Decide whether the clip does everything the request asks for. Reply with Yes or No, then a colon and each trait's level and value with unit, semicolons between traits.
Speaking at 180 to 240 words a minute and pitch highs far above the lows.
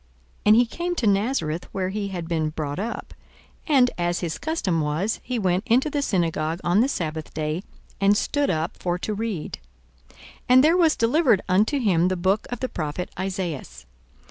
Yes: average, 190 wpm; wide, 6.3 semitones